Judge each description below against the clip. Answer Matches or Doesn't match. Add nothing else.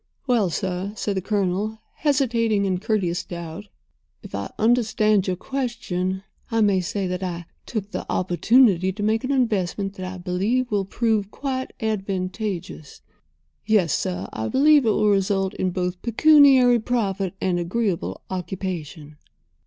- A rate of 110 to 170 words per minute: Matches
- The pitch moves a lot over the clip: Doesn't match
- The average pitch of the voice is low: Doesn't match